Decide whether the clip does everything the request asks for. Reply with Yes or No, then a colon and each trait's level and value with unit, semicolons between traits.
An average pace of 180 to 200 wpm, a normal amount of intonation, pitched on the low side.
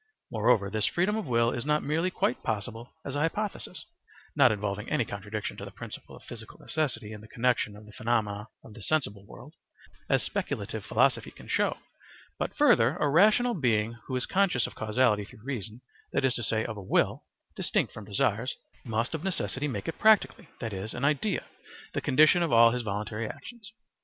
No: average, 190 wpm; wide, 6.0 semitones; low, 120 Hz